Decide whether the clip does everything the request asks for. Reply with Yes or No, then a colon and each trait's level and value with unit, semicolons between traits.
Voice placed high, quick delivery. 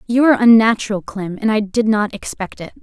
Yes: high, 215 Hz; fast, 215 wpm